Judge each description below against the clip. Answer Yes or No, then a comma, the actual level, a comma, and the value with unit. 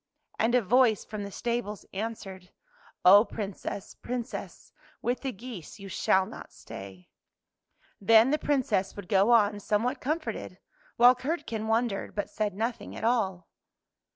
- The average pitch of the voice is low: No, high, 220 Hz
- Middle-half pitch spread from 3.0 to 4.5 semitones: Yes, average, 3.6 semitones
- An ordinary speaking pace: Yes, average, 150 wpm